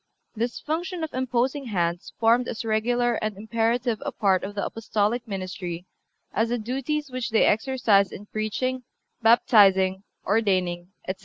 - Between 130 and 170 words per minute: Yes, average, 145 wpm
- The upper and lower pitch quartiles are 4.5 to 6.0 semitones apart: No, average, 3.7 semitones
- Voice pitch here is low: No, high, 225 Hz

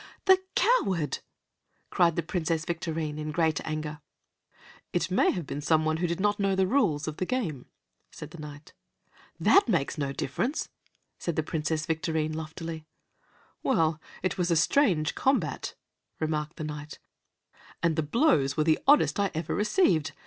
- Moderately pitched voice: Yes, medium, 160 Hz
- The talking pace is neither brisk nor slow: Yes, average, 155 wpm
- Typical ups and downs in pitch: Yes, average, 3.3 semitones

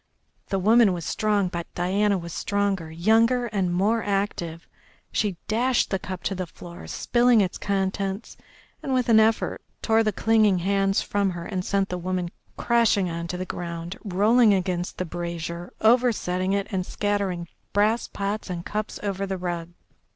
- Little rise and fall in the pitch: No, average, 3.2 semitones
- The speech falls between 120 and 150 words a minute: No, average, 165 wpm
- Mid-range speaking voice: No, high, 195 Hz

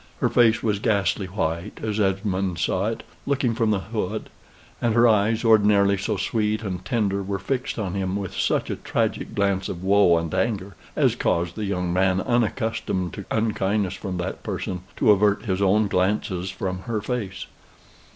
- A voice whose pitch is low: Yes, low, 100 Hz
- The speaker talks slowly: No, average, 175 wpm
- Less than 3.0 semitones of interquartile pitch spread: Yes, narrow, 2.6 semitones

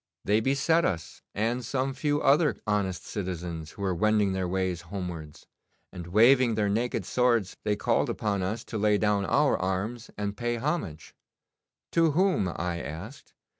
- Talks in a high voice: No, low, 105 Hz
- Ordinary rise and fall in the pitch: Yes, average, 5.0 semitones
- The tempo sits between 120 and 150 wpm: No, average, 160 wpm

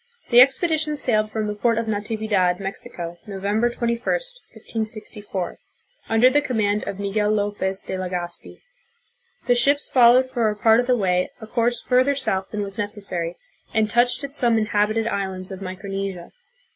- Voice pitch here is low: No, high, 215 Hz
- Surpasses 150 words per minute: Yes, average, 160 wpm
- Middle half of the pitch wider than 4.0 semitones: No, average, 3.5 semitones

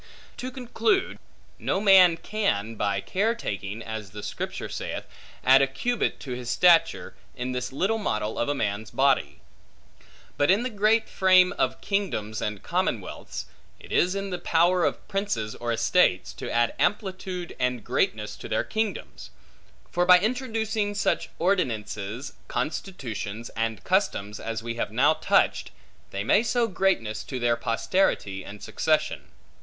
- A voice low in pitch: No, medium, 145 Hz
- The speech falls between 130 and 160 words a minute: Yes, average, 150 wpm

